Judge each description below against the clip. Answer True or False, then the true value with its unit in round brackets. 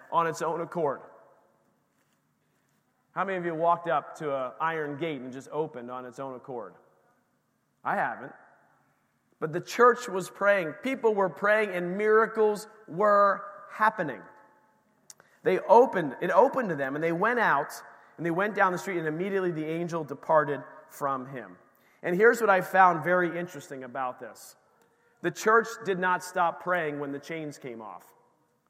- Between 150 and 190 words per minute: True (165 wpm)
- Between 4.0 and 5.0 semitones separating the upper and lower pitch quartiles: True (4.6 semitones)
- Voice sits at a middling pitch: True (175 Hz)